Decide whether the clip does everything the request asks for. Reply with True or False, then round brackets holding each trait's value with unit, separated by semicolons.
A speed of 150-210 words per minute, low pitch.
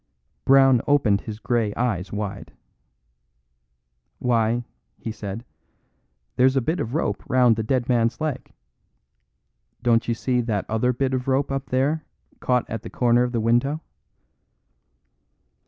False (140 wpm; 120 Hz)